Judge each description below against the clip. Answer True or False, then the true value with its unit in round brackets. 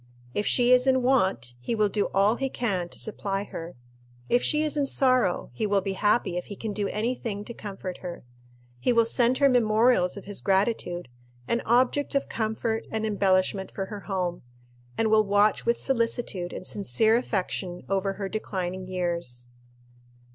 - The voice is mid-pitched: False (205 Hz)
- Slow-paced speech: False (180 wpm)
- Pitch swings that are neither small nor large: True (4.0 semitones)